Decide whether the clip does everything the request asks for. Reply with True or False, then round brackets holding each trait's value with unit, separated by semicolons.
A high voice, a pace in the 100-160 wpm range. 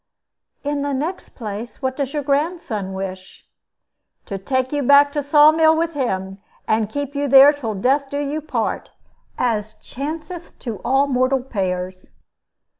True (270 Hz; 155 wpm)